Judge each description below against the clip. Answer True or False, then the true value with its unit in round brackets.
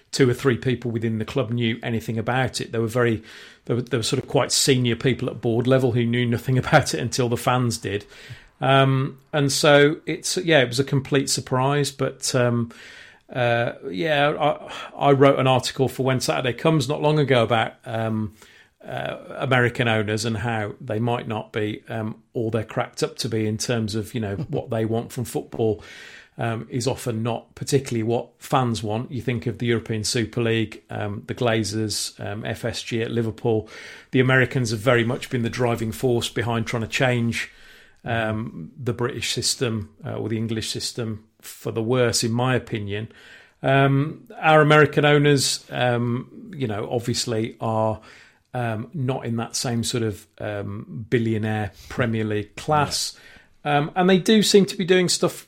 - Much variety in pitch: False (2.9 semitones)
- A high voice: False (120 Hz)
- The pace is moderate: True (185 wpm)